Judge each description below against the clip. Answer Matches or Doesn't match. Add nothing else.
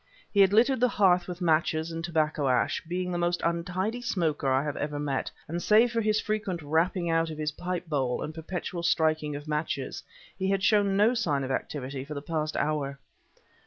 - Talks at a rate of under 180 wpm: Doesn't match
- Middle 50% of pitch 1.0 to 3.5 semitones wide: Doesn't match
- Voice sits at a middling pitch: Matches